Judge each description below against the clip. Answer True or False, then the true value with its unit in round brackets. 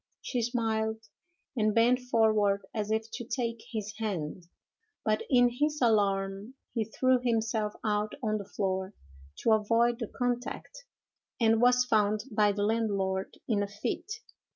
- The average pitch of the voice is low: False (220 Hz)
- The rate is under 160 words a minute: True (145 wpm)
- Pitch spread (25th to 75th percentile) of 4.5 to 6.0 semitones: False (2.5 semitones)